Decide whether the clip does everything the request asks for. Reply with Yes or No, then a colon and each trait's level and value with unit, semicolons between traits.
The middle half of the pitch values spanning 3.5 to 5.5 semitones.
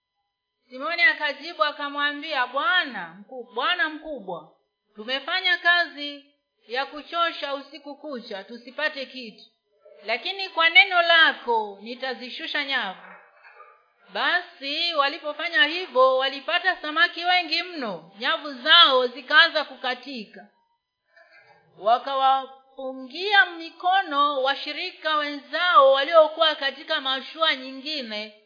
Yes: average, 4.3 semitones